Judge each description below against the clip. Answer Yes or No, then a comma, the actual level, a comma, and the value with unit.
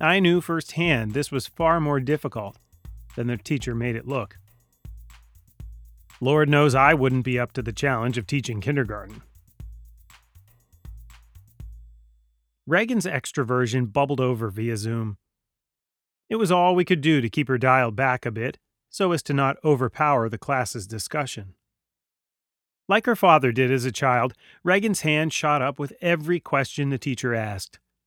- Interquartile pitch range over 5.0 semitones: Yes, wide, 5.5 semitones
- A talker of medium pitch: No, low, 125 Hz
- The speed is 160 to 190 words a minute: No, average, 150 wpm